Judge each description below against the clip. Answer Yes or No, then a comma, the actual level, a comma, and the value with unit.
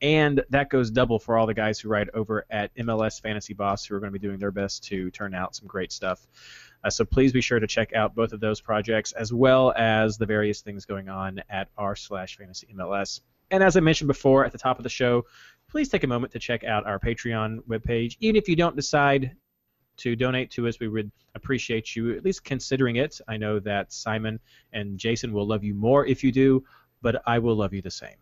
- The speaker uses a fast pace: Yes, fast, 240 wpm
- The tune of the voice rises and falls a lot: No, average, 3.5 semitones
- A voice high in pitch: No, low, 115 Hz